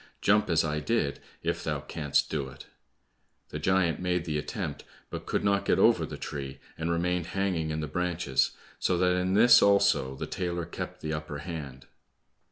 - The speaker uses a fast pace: No, average, 180 wpm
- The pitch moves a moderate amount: Yes, average, 3.3 semitones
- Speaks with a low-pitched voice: Yes, very low, 85 Hz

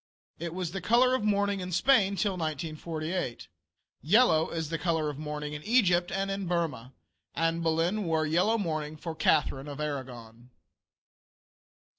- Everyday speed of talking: Yes, average, 150 wpm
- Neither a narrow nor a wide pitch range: Yes, average, 4.2 semitones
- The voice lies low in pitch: No, medium, 165 Hz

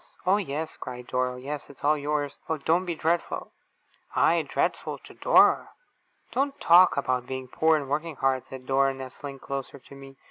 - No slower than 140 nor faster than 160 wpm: No, average, 180 wpm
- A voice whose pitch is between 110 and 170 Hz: Yes, medium, 140 Hz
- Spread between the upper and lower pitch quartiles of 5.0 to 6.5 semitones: No, average, 3.2 semitones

